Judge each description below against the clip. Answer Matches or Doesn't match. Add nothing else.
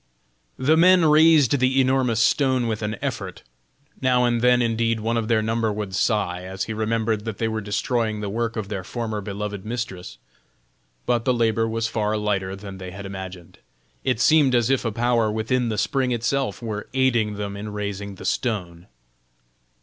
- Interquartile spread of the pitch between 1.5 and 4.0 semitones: Matches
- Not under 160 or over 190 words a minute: Matches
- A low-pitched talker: Matches